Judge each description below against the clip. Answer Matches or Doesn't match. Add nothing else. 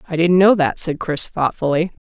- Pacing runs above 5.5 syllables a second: Doesn't match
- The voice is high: Doesn't match